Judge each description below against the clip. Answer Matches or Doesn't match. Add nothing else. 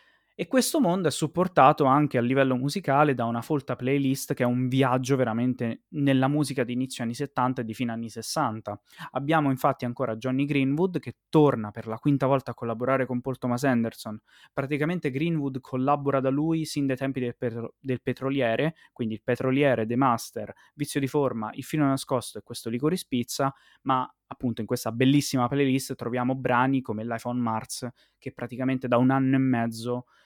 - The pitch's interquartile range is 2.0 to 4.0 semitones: Matches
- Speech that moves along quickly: Matches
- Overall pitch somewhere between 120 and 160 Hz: Matches